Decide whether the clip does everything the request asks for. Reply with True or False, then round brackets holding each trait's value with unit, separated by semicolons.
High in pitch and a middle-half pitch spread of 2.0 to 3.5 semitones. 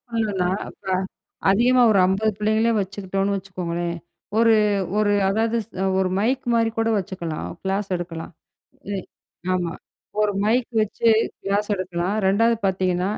True (195 Hz; 3.1 semitones)